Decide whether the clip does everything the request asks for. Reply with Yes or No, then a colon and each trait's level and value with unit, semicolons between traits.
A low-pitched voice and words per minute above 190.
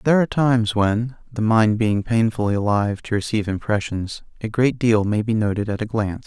Yes: low, 110 Hz; average, 200 wpm